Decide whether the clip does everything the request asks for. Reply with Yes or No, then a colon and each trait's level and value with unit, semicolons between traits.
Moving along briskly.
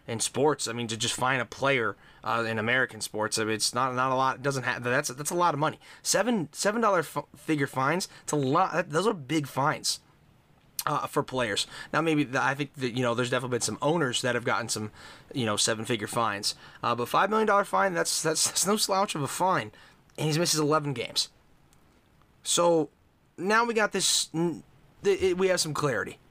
Yes: fast, 220 wpm